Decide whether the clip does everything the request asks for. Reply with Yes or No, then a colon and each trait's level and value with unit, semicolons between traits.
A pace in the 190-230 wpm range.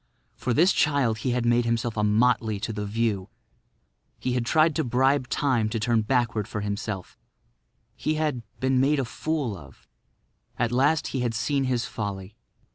No: average, 170 wpm